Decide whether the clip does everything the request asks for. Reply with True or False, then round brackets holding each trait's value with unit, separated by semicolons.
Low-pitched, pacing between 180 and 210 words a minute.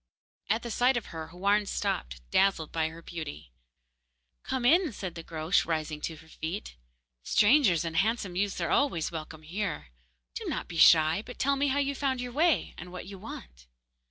False (180 Hz; 185 wpm)